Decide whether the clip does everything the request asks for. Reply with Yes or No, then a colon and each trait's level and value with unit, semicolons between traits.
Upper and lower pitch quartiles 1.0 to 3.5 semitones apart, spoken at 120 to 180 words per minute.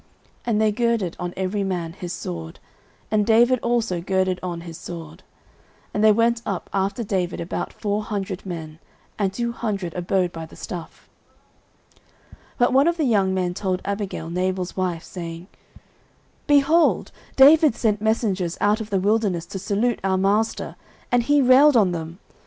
No: average, 4.2 semitones; average, 165 wpm